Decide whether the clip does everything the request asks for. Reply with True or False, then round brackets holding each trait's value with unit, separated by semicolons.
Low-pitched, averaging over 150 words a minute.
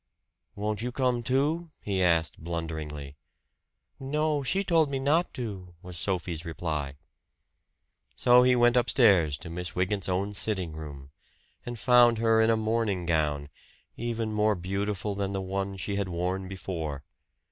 False (100 Hz; 145 wpm)